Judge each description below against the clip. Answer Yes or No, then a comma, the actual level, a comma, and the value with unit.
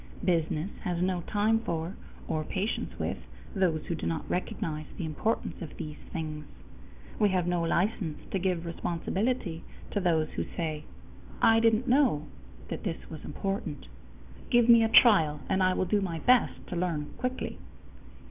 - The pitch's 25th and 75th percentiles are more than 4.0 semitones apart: Yes, average, 4.5 semitones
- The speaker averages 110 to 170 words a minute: Yes, average, 160 wpm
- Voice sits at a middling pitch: Yes, medium, 180 Hz